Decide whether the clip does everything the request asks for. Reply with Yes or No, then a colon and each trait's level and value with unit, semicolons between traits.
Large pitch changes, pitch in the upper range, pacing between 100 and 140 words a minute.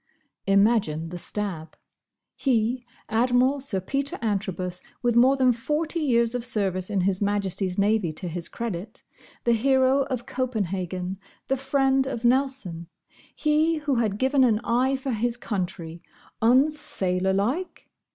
Yes: wide, 5.7 semitones; high, 230 Hz; slow, 135 wpm